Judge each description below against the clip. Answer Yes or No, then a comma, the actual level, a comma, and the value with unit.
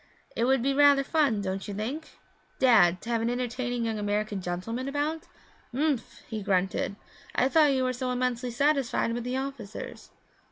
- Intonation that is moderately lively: Yes, average, 4.2 semitones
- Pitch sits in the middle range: No, high, 245 Hz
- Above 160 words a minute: Yes, average, 170 wpm